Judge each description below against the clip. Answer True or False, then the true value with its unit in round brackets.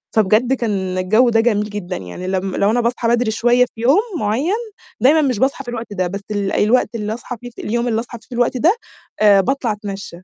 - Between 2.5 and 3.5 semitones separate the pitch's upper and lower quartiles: True (3.1 semitones)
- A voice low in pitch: False (225 Hz)